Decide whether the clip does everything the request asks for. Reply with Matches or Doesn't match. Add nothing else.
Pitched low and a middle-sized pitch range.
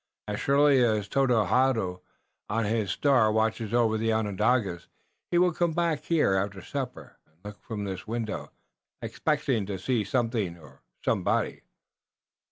Matches